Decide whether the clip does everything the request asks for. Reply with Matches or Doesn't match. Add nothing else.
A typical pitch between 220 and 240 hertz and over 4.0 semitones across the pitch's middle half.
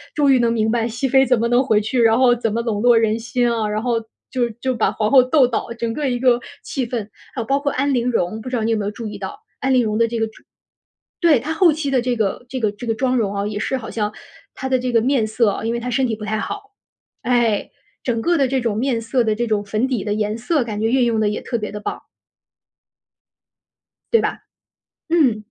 Doesn't match